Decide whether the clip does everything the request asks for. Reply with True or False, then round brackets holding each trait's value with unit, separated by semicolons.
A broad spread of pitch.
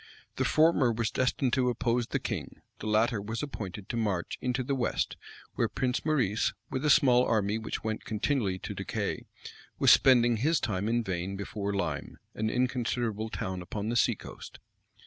False (3.3 semitones)